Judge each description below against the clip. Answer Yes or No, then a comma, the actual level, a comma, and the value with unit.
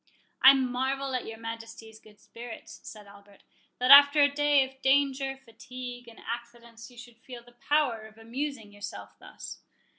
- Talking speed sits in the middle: Yes, average, 160 wpm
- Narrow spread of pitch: No, average, 3.0 semitones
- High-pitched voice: Yes, high, 245 Hz